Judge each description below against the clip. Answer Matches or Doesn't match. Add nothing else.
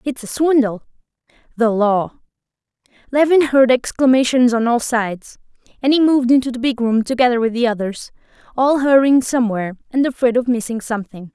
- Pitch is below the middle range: Doesn't match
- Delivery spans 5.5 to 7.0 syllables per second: Matches